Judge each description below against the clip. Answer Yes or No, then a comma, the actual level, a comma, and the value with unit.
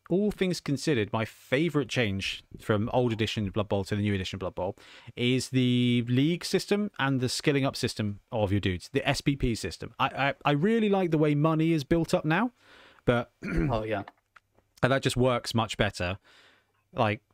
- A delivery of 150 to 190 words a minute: Yes, average, 185 wpm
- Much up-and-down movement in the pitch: Yes, wide, 6.9 semitones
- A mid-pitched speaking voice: No, low, 130 Hz